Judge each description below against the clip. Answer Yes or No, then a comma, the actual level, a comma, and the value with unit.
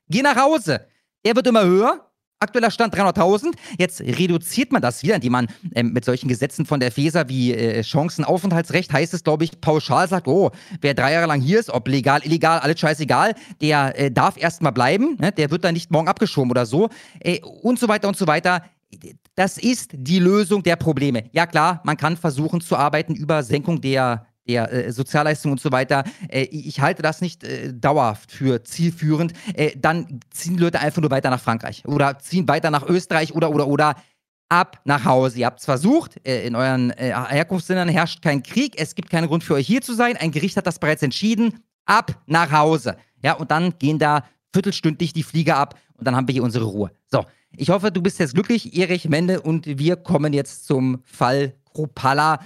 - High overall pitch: No, medium, 155 Hz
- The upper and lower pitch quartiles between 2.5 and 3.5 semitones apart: No, average, 4.7 semitones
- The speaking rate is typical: No, fast, 205 wpm